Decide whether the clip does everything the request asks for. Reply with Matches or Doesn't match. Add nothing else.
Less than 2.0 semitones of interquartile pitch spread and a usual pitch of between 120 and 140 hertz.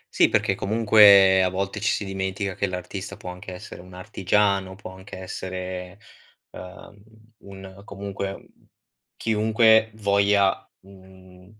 Doesn't match